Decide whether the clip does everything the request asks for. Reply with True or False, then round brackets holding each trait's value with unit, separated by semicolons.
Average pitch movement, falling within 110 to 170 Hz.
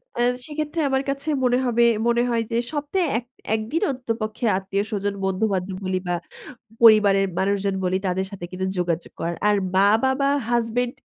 False (4.4 semitones; 215 Hz)